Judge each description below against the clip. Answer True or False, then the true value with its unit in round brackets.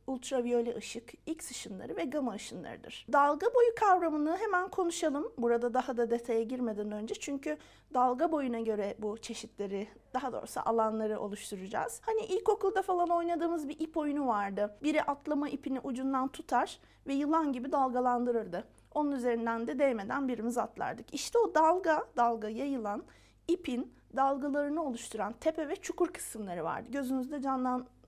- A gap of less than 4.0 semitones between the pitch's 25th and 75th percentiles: False (5.1 semitones)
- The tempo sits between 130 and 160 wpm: True (140 wpm)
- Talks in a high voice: True (265 Hz)